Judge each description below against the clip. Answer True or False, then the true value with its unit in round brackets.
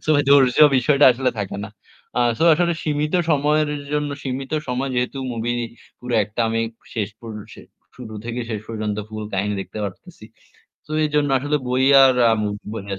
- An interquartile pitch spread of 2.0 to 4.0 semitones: False (4.6 semitones)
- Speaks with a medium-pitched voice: False (125 Hz)